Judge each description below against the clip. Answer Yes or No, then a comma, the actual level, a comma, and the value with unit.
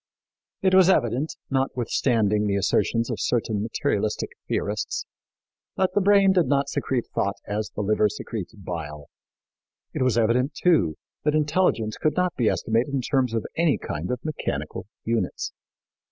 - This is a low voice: Yes, low, 120 Hz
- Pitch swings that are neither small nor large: No, wide, 6.1 semitones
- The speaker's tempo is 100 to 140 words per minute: No, average, 150 wpm